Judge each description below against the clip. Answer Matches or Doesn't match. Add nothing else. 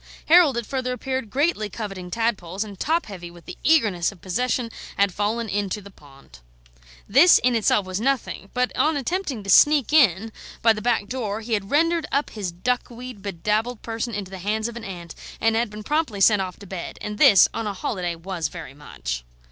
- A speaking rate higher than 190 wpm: Matches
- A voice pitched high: Matches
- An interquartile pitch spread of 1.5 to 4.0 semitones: Doesn't match